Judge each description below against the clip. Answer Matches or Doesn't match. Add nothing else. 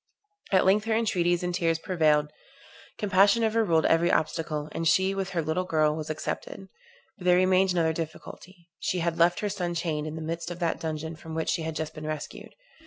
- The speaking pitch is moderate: Matches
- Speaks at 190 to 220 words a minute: Matches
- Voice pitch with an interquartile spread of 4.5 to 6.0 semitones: Doesn't match